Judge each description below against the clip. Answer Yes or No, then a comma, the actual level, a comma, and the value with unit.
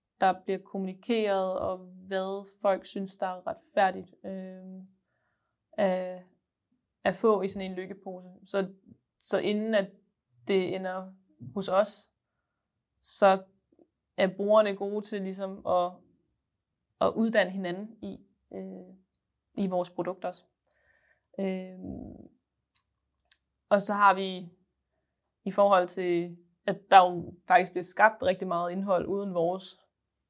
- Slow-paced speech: Yes, slow, 120 wpm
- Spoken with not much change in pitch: Yes, narrow, 1.4 semitones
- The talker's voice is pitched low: No, high, 190 Hz